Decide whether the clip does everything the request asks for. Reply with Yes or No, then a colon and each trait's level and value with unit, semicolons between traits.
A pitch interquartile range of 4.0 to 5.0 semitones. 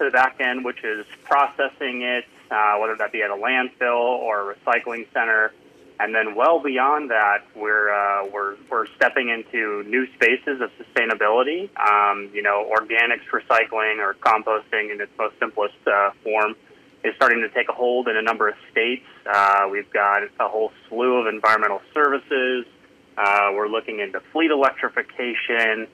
No: average, 3.2 semitones